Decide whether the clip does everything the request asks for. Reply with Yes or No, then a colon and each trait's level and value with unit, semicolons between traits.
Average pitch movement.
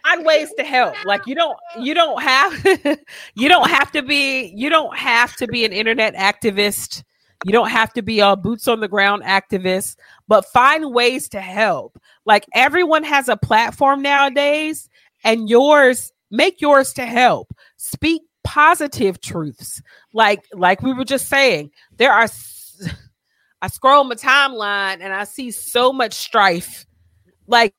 No: wide, 6.0 semitones